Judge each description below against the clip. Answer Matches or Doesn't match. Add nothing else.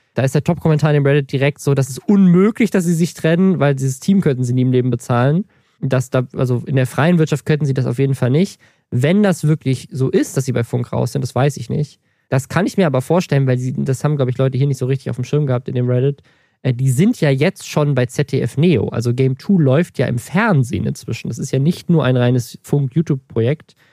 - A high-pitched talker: Doesn't match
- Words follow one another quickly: Matches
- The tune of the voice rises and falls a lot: Doesn't match